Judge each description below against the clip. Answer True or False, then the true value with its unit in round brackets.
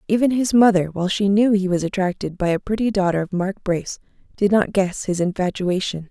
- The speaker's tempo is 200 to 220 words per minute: True (205 wpm)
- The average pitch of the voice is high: True (195 Hz)